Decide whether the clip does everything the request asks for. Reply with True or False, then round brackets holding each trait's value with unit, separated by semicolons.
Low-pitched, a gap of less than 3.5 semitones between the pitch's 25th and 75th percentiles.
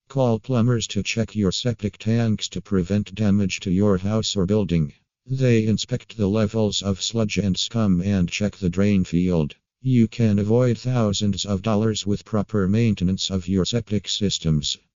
True (105 Hz; 2.8 semitones)